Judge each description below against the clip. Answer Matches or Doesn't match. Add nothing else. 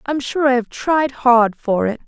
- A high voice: Matches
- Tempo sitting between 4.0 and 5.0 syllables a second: Matches